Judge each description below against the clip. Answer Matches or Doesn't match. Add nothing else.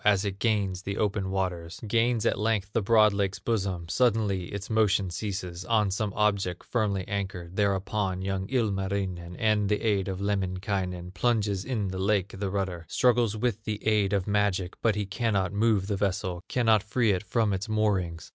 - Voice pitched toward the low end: Matches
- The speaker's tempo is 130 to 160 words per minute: Doesn't match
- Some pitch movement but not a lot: Doesn't match